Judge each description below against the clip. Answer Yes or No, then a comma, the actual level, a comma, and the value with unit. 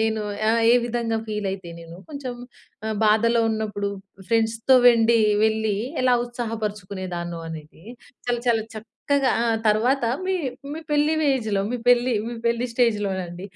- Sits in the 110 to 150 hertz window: No, high, 225 Hz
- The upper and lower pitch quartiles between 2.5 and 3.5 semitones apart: Yes, average, 2.8 semitones